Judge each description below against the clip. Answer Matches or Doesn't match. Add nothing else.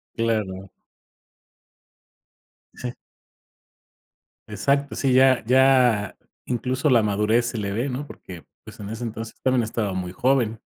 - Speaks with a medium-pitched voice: Doesn't match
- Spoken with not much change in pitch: Doesn't match